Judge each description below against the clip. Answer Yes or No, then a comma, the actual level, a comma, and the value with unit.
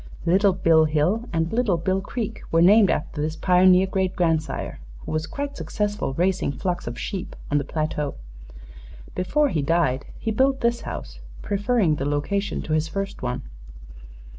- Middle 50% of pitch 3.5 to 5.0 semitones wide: Yes, average, 4.6 semitones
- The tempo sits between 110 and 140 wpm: No, average, 165 wpm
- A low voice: No, medium, 180 Hz